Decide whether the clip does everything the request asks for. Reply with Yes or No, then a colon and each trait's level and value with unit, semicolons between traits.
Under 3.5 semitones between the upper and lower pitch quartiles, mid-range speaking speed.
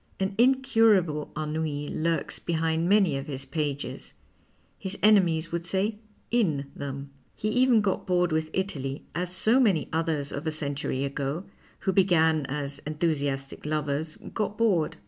No: average, 4.8 semitones; average, 145 wpm